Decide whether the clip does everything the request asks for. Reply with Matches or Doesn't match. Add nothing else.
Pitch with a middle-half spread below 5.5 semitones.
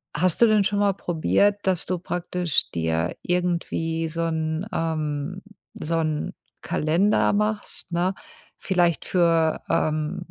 Matches